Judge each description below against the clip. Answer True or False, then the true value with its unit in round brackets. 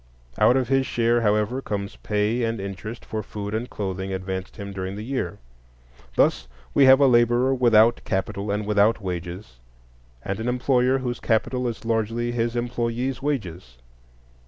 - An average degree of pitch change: True (3.4 semitones)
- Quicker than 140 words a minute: True (160 wpm)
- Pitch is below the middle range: True (115 Hz)